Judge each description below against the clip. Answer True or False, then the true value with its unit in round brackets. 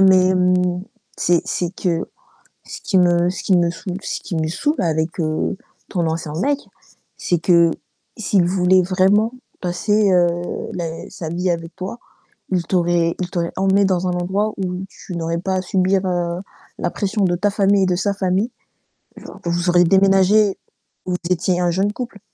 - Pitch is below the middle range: False (180 Hz)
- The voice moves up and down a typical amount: False (1.8 semitones)